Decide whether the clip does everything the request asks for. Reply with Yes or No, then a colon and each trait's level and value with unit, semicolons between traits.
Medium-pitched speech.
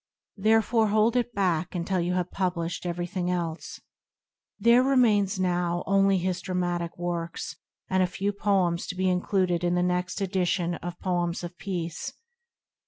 Yes: medium, 180 Hz